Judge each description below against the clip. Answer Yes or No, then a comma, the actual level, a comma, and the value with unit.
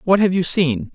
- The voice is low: No, medium, 165 Hz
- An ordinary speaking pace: No, fast, 255 wpm